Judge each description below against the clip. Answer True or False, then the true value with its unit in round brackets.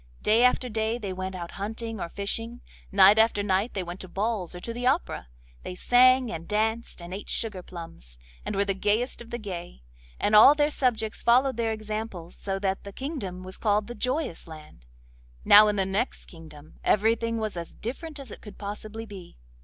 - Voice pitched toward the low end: False (210 Hz)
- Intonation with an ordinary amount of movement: True (3.7 semitones)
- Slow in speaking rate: False (200 wpm)